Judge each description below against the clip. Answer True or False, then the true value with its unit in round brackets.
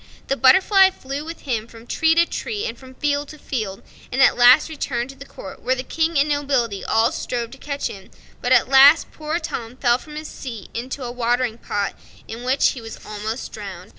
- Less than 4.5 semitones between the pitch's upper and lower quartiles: True (3.7 semitones)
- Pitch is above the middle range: True (260 Hz)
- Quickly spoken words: True (210 wpm)